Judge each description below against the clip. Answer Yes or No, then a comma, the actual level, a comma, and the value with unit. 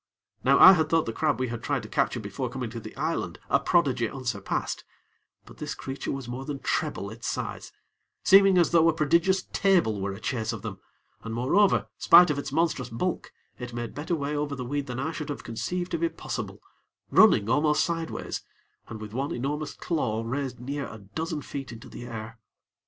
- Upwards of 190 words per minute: Yes, average, 200 wpm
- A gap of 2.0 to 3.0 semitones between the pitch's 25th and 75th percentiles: No, wide, 5.4 semitones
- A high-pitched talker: No, low, 135 Hz